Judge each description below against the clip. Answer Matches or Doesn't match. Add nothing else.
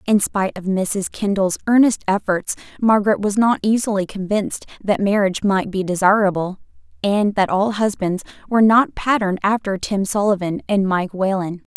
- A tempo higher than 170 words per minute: Doesn't match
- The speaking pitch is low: Doesn't match